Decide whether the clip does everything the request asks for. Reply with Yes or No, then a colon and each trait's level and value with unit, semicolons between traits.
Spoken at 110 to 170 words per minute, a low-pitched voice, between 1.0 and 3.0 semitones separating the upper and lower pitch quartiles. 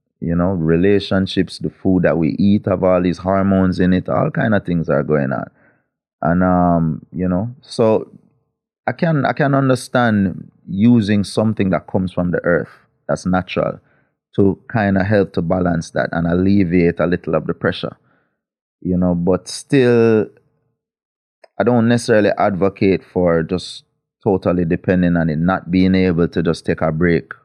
Yes: average, 165 wpm; very low, 95 Hz; narrow, 2.6 semitones